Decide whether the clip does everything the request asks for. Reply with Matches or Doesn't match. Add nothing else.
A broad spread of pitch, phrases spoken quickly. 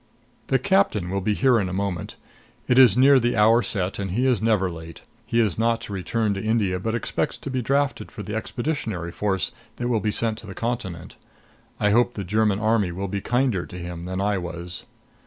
Doesn't match